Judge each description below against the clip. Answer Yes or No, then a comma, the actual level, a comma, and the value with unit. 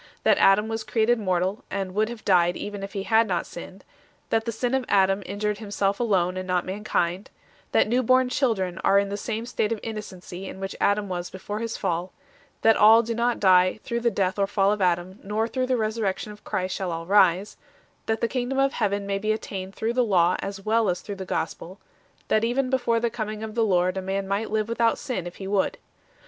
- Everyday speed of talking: No, fast, 230 wpm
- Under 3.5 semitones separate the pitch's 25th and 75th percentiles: Yes, average, 3.0 semitones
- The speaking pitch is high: Yes, high, 205 Hz